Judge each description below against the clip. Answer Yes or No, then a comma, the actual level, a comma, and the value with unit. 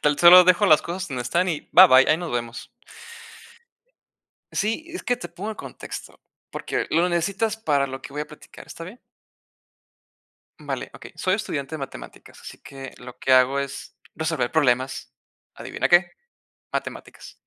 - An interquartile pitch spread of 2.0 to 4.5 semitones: No, average, 5.2 semitones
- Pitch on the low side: No, medium, 160 Hz